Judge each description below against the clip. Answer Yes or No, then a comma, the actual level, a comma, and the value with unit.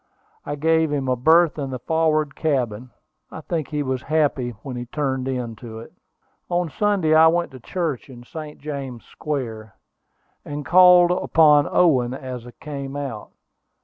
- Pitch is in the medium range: Yes, medium, 145 Hz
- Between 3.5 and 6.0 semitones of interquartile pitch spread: Yes, average, 3.9 semitones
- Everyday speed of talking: Yes, average, 160 wpm